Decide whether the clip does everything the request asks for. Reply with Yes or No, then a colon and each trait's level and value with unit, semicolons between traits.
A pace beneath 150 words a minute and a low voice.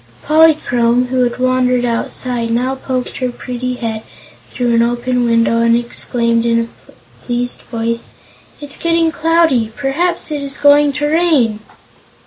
No: average, 140 wpm; very high, 250 Hz